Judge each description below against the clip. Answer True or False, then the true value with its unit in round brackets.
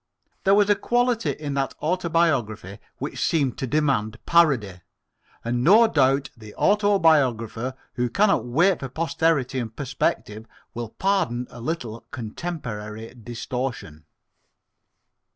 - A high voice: False (135 Hz)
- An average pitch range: False (6.6 semitones)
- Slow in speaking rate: True (115 wpm)